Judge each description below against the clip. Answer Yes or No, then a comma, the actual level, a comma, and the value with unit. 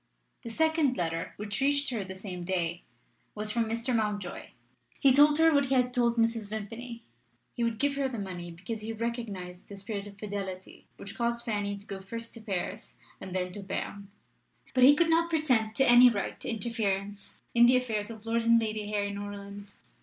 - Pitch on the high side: Yes, high, 220 Hz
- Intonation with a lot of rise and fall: No, average, 3.3 semitones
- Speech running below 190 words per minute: No, average, 200 wpm